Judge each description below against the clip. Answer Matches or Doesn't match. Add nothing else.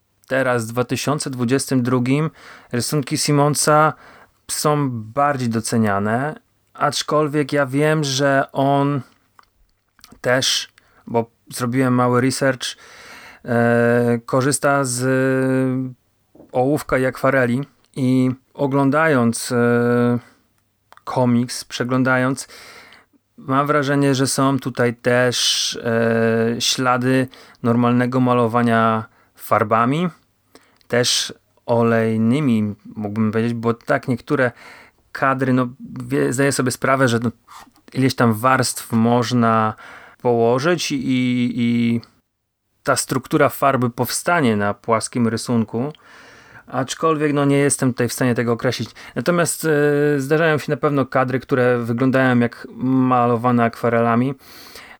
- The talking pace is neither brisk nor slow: Doesn't match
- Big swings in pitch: Doesn't match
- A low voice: Matches